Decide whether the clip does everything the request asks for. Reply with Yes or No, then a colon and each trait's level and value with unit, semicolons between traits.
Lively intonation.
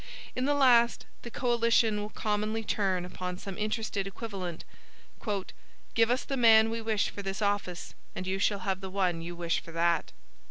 No: average, 3.5 semitones